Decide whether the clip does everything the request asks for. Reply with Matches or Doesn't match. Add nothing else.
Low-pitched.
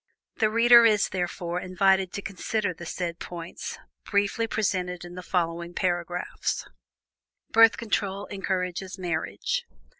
Doesn't match